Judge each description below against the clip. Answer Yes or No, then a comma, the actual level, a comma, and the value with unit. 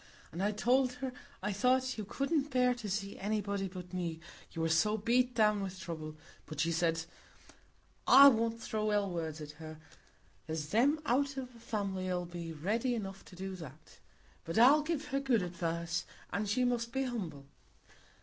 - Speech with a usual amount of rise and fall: No, wide, 6.4 semitones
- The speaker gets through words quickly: No, average, 180 wpm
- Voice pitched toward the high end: Yes, high, 205 Hz